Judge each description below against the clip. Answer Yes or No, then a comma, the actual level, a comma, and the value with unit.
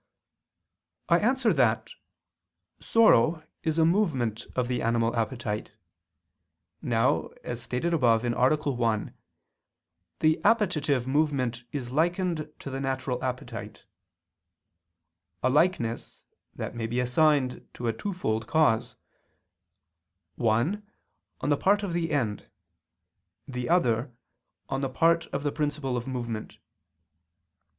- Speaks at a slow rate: Yes, slow, 115 wpm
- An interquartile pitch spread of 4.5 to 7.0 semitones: Yes, average, 5.1 semitones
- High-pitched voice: No, low, 130 Hz